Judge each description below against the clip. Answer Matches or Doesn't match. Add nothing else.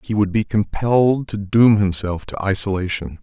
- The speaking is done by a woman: Doesn't match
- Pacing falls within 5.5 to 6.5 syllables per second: Doesn't match